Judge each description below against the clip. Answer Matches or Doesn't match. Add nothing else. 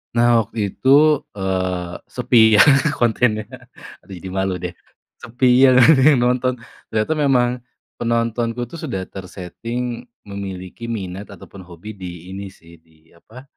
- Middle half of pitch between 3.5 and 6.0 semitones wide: Matches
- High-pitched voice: Doesn't match